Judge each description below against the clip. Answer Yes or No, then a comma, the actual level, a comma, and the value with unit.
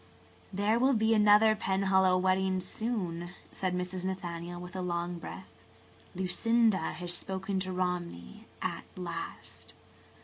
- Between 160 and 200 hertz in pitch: Yes, medium, 185 Hz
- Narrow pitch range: Yes, narrow, 2.1 semitones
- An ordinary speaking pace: No, slow, 130 wpm